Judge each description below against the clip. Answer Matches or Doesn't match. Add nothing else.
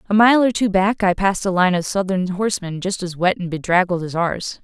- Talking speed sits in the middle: Doesn't match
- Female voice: Matches